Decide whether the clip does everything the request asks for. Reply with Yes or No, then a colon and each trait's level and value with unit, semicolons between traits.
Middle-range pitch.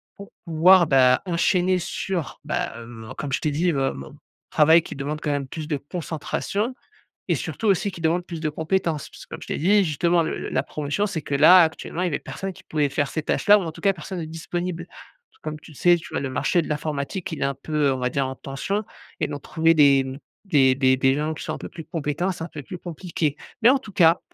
Yes: medium, 160 Hz